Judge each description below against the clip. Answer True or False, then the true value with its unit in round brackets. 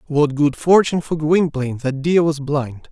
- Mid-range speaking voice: True (150 Hz)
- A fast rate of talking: False (185 wpm)